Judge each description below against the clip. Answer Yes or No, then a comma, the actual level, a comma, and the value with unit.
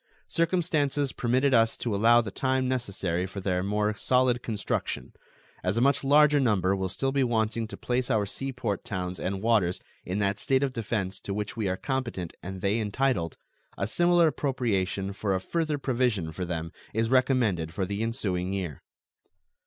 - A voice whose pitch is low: Yes, low, 110 Hz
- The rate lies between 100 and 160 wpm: No, average, 175 wpm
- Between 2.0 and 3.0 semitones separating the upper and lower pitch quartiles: No, average, 5.3 semitones